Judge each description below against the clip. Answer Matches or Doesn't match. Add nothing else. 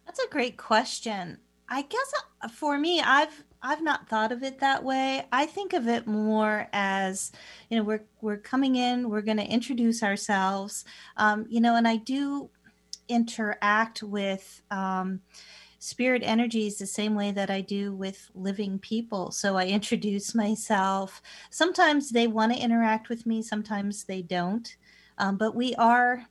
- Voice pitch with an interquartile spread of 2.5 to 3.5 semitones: Matches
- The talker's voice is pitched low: Doesn't match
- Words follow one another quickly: Doesn't match